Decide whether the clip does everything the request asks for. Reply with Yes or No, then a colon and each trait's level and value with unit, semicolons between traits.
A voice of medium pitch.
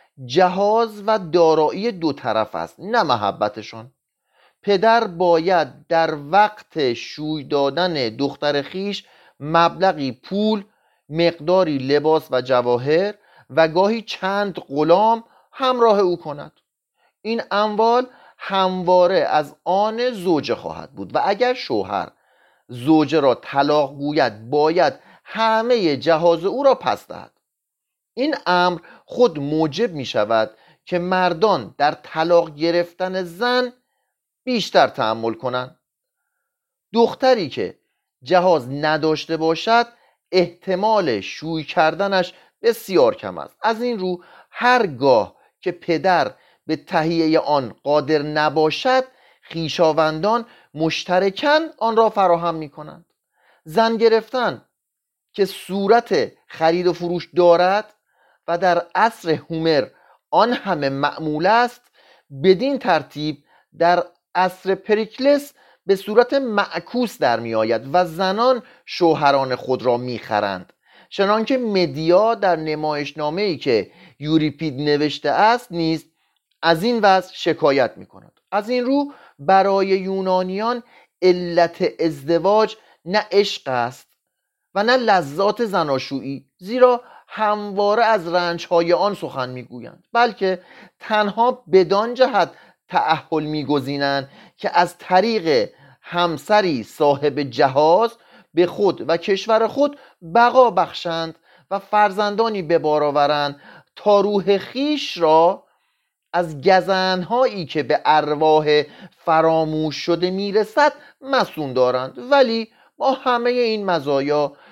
Yes: medium, 180 Hz